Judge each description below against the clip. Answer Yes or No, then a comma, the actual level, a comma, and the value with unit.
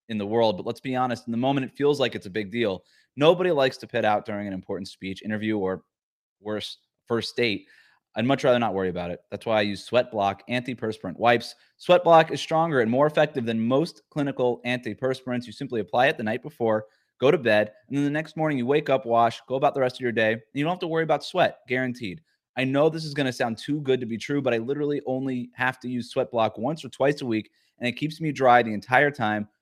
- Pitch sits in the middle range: No, low, 125 Hz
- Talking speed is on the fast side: Yes, fast, 255 wpm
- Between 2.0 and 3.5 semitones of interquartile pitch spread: No, average, 4.1 semitones